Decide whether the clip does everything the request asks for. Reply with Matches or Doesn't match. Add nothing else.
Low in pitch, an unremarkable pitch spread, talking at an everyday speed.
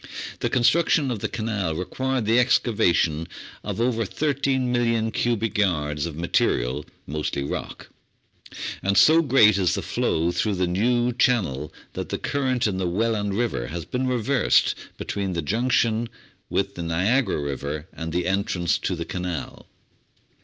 Doesn't match